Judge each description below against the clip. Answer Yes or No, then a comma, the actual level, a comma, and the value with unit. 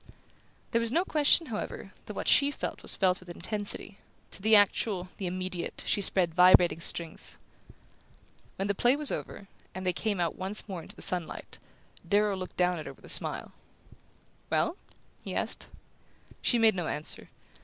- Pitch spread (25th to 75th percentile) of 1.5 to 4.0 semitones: Yes, average, 3.4 semitones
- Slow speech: No, average, 175 wpm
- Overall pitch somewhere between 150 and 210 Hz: Yes, high, 190 Hz